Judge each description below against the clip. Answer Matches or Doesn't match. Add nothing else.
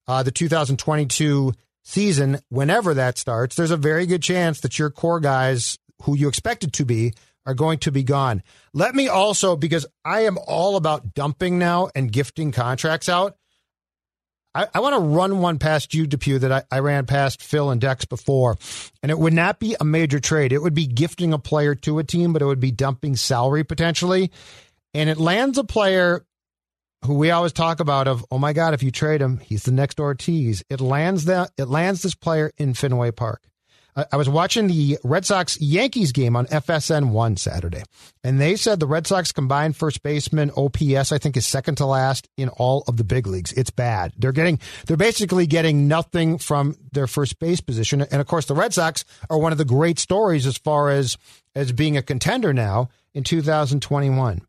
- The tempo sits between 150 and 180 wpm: Doesn't match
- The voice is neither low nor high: Matches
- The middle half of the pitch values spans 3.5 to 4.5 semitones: Matches